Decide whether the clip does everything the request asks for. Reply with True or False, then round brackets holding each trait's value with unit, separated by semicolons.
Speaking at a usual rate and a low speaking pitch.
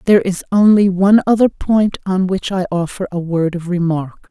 False (195 wpm; 185 Hz)